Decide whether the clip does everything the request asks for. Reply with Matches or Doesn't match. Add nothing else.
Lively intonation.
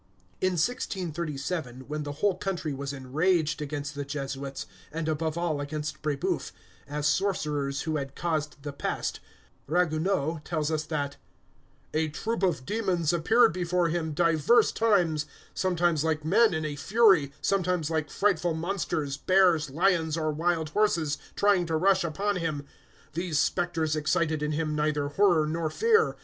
Doesn't match